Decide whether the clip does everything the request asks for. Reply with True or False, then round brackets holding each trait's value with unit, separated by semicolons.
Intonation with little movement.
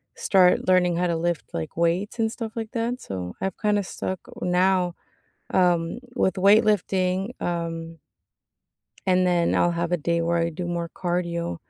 True (2.2 semitones)